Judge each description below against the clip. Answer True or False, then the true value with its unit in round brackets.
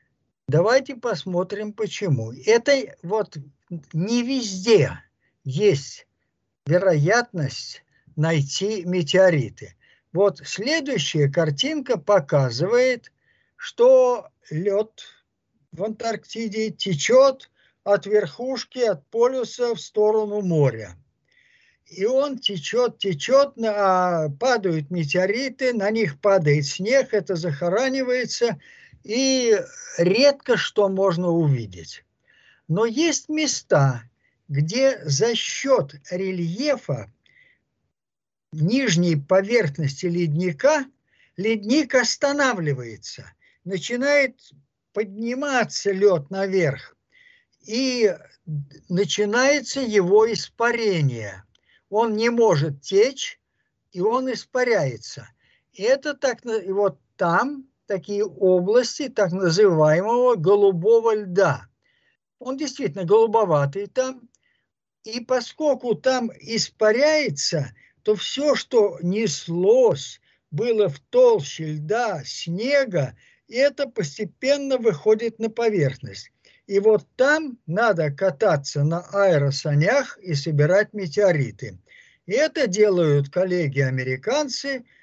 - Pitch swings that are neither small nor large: False (7.3 semitones)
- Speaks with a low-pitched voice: False (210 Hz)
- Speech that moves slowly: True (85 wpm)